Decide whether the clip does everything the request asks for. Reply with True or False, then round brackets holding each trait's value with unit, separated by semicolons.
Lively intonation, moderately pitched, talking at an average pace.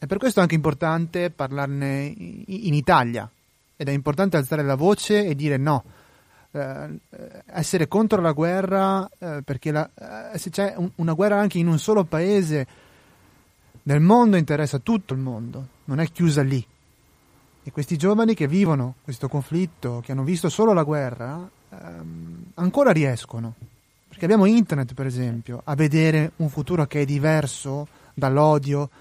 False (4.9 semitones; 155 Hz; 155 wpm)